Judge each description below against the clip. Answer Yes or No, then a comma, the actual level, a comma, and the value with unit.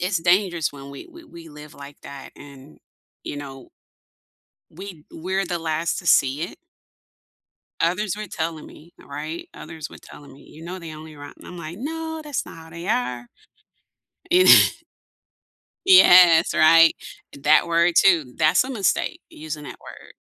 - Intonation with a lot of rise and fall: No, average, 3.6 semitones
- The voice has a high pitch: No, medium, 165 Hz